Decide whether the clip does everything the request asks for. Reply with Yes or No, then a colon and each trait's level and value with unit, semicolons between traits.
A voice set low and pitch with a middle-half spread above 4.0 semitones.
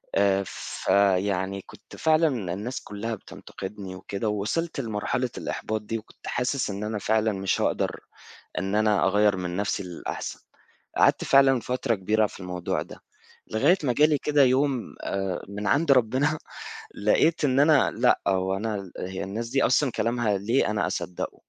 Yes: low, 105 Hz; average, 4.7 semitones